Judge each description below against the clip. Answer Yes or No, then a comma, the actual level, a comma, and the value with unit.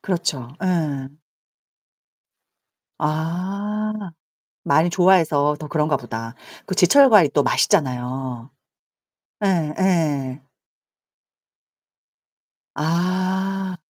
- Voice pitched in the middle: Yes, medium, 165 Hz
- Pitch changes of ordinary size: Yes, average, 4.8 semitones